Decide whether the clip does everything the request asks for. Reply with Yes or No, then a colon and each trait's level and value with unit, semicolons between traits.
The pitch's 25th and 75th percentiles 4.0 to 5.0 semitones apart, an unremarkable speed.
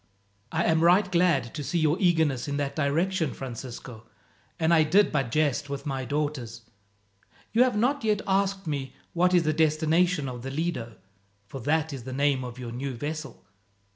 Yes: average, 4.4 semitones; average, 180 wpm